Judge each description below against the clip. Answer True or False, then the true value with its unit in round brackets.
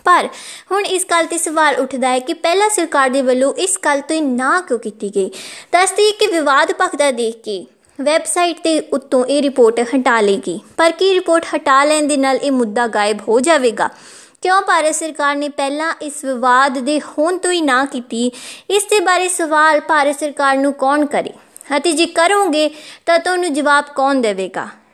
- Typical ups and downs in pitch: True (4.1 semitones)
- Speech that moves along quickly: True (190 wpm)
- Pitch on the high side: True (295 Hz)